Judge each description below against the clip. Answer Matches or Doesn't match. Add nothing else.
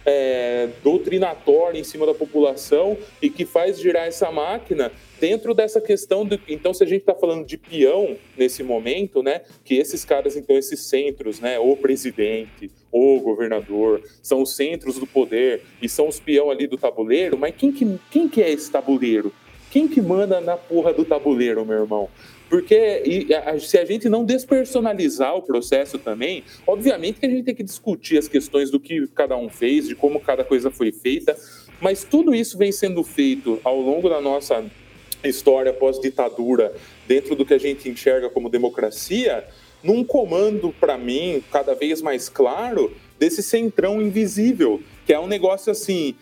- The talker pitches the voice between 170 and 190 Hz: Matches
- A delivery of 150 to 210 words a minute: Matches